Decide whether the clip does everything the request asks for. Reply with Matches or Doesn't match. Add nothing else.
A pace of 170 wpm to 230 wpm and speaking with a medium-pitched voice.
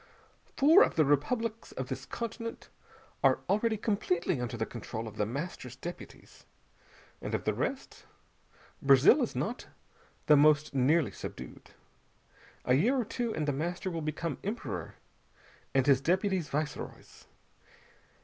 Doesn't match